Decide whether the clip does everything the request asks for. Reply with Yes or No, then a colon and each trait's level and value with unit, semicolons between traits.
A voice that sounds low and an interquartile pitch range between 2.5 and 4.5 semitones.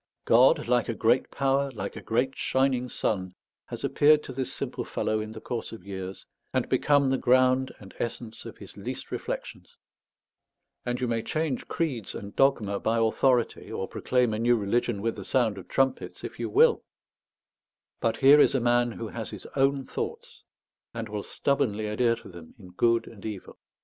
Yes: low, 120 Hz; average, 3.5 semitones